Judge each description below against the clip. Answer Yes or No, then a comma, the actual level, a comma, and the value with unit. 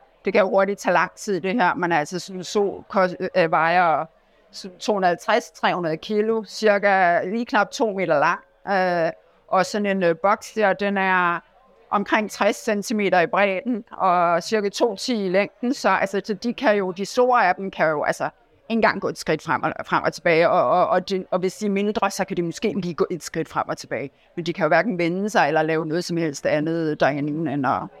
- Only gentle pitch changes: No, average, 3.2 semitones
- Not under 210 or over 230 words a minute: Yes, fast, 225 wpm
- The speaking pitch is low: No, high, 195 Hz